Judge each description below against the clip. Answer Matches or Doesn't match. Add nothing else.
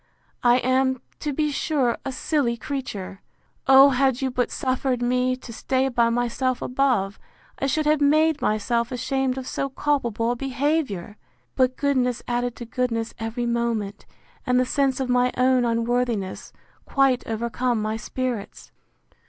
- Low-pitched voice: Doesn't match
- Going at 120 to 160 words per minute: Matches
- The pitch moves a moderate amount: Doesn't match